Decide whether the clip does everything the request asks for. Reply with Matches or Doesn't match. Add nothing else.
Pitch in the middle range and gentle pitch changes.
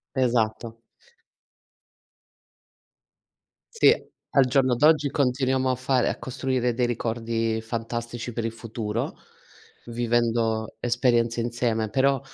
Doesn't match